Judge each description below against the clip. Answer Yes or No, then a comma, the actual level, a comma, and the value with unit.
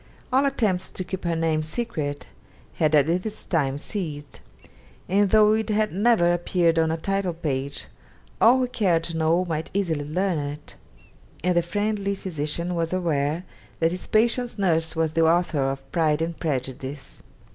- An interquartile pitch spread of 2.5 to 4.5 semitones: Yes, average, 4.1 semitones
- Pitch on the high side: No, medium, 170 Hz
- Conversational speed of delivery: Yes, average, 165 wpm